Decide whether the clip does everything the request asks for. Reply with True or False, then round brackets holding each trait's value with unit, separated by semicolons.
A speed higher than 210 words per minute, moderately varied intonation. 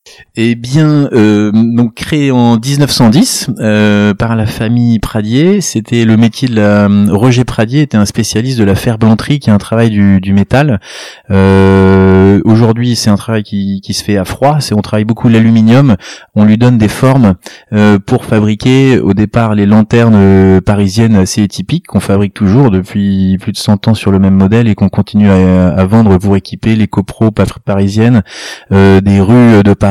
False (185 wpm; 3.0 semitones)